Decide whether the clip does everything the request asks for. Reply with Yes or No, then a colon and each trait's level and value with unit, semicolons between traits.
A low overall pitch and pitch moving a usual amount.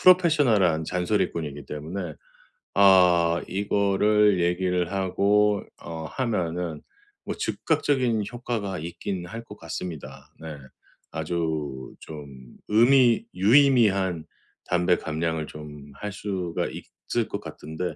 Yes: very low, 90 Hz; average, 4.4 semitones